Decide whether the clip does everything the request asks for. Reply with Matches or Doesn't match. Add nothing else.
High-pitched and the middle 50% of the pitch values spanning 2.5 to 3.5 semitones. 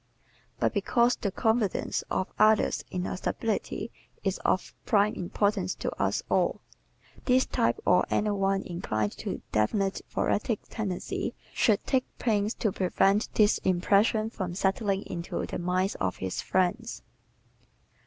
Matches